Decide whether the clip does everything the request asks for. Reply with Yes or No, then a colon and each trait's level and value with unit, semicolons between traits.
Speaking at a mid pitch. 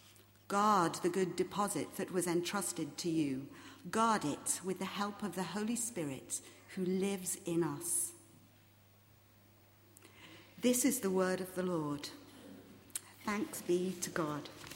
Yes: medium, 175 Hz